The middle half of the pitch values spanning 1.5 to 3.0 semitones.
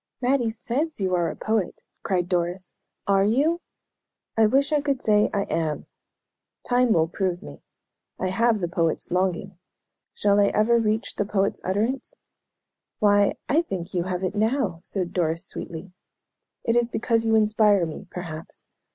No: average, 4.2 semitones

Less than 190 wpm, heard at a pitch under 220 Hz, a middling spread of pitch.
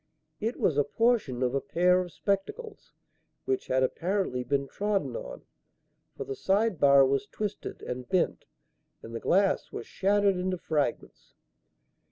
No: average, 150 wpm; medium, 185 Hz; wide, 7.0 semitones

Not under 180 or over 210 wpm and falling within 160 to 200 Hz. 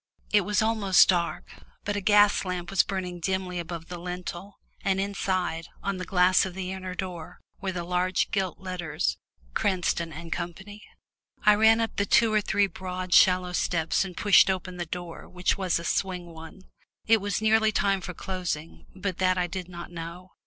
Yes: average, 185 wpm; medium, 185 Hz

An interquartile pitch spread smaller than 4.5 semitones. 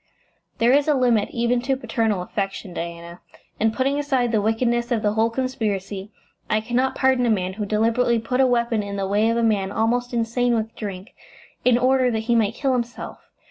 Yes: average, 2.9 semitones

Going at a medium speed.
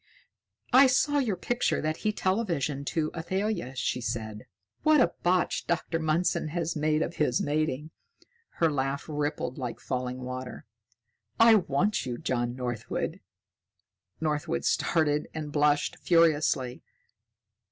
No: slow, 125 wpm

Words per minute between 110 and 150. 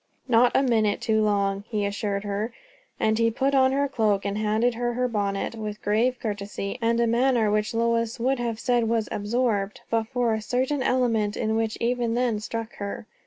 No: average, 200 wpm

